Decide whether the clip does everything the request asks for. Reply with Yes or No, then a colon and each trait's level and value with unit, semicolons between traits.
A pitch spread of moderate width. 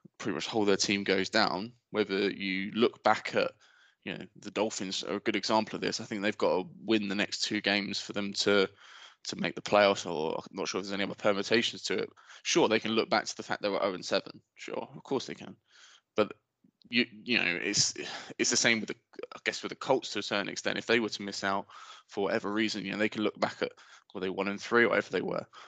No: narrow, 1.5 semitones